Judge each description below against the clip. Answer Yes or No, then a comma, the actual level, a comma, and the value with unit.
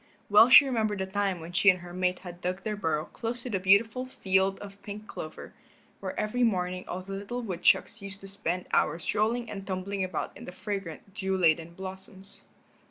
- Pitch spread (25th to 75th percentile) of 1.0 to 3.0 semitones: Yes, narrow, 2.5 semitones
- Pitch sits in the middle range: No, high, 195 Hz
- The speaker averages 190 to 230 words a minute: Yes, average, 200 wpm